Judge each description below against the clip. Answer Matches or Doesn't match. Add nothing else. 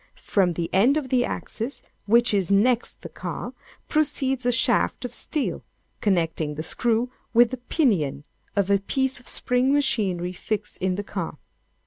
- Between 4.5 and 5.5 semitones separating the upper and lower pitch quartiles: Matches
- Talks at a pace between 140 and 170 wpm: Matches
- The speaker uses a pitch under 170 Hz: Doesn't match